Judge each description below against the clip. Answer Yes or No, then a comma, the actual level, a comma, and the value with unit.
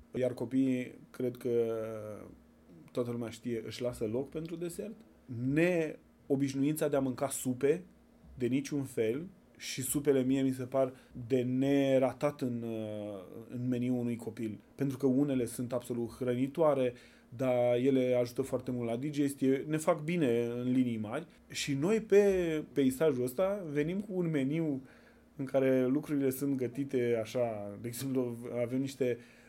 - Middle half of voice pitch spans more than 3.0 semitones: No, average, 2.7 semitones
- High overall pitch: No, low, 130 Hz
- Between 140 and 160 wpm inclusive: Yes, average, 145 wpm